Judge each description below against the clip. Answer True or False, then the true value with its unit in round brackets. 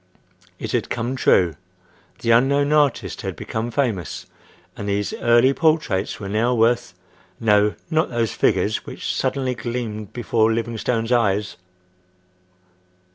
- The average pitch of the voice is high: False (115 Hz)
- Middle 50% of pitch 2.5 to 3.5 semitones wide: True (2.9 semitones)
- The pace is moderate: False (120 wpm)